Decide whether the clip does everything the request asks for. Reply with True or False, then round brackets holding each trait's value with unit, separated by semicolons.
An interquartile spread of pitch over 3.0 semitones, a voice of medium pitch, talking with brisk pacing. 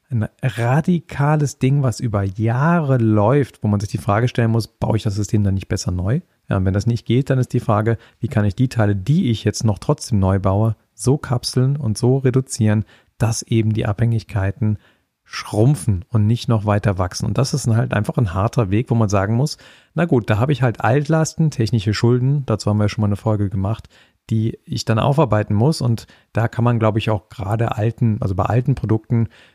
False (3.4 semitones; 115 Hz; 215 wpm)